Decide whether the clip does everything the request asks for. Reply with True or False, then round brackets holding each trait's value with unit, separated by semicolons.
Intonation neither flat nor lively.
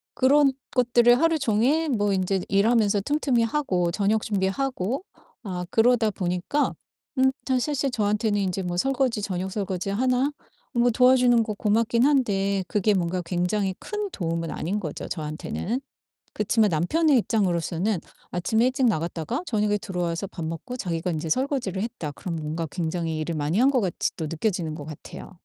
False (5.7 semitones)